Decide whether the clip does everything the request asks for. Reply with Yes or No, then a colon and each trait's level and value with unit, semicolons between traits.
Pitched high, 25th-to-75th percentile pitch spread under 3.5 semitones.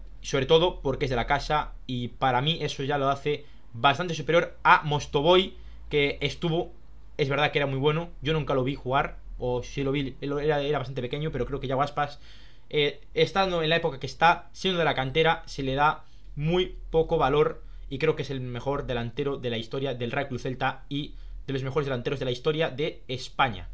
No: medium, 140 Hz; average, 3.0 semitones